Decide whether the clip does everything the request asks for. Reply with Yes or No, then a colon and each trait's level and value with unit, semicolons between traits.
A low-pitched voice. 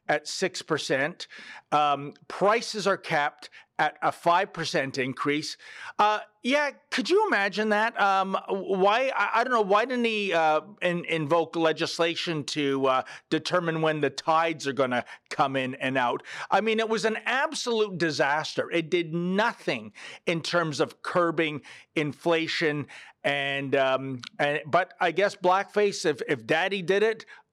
No: medium, 170 Hz